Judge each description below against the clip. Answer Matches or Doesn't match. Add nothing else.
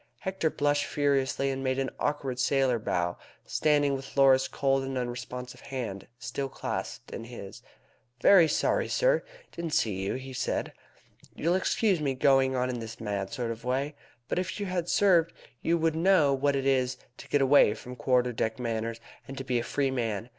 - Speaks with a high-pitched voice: Doesn't match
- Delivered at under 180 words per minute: Doesn't match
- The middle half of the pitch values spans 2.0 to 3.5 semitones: Matches